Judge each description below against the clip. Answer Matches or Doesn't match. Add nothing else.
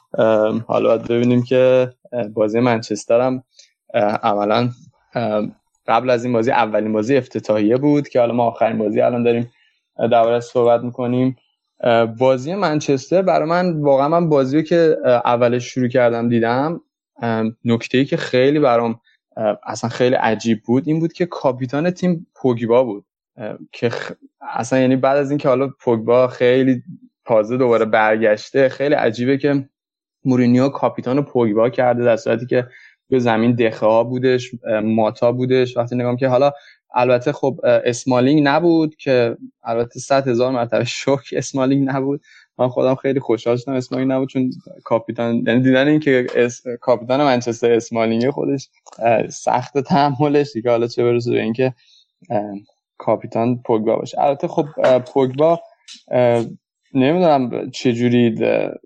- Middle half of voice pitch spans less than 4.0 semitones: Matches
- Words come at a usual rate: Matches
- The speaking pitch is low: Matches